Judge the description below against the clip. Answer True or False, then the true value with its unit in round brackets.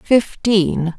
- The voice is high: True (195 Hz)